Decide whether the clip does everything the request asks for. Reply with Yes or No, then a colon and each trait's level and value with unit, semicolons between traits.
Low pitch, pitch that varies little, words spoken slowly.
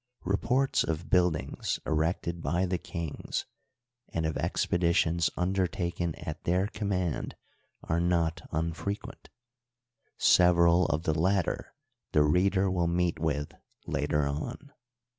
Yes: very low, 85 Hz; narrow, 2.3 semitones; slow, 115 wpm